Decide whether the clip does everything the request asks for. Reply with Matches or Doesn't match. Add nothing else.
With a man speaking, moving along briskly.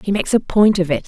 Doesn't match